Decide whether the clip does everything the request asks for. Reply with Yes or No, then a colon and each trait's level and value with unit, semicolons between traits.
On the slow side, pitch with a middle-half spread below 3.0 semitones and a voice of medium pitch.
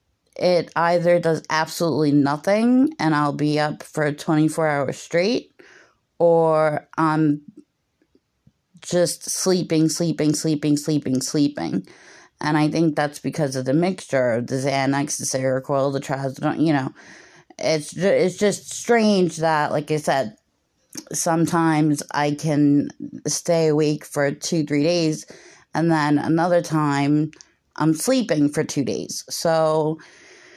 Yes: slow, 130 wpm; narrow, 2.4 semitones; medium, 155 Hz